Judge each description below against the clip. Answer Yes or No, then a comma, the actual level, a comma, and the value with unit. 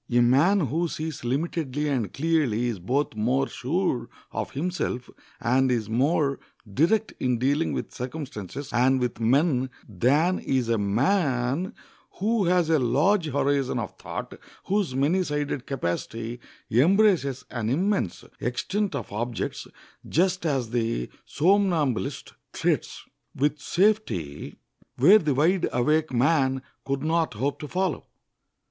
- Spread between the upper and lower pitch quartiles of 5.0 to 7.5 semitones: Yes, average, 5.3 semitones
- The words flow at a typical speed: No, slow, 130 wpm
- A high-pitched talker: No, medium, 140 Hz